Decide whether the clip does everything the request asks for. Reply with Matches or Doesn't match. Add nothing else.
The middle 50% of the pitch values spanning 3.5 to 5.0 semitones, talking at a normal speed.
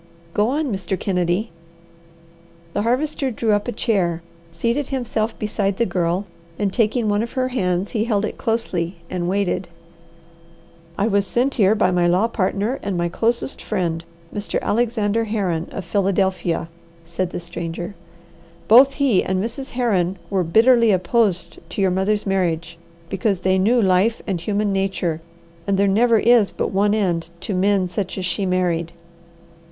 Matches